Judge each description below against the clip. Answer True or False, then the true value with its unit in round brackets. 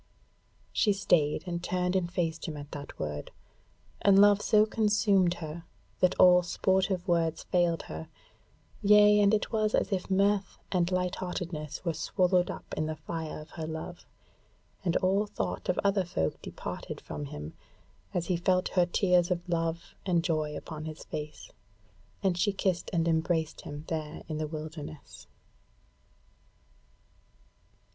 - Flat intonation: False (3.2 semitones)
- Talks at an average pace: True (150 wpm)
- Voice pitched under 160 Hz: False (175 Hz)